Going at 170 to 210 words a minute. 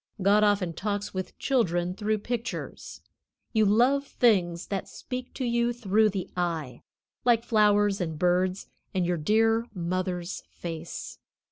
No: slow, 135 wpm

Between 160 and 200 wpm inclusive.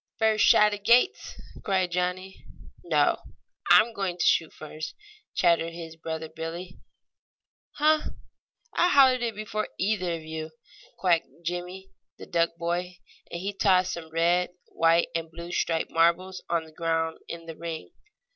No: average, 145 wpm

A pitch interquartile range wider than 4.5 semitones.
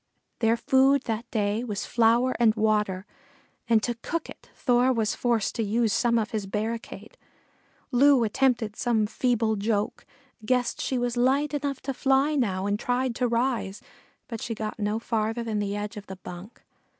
No: average, 2.8 semitones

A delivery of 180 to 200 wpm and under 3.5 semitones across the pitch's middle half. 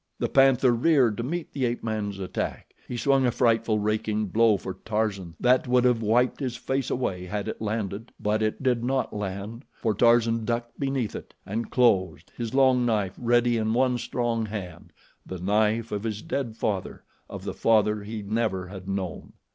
Yes: average, 185 wpm; average, 2.8 semitones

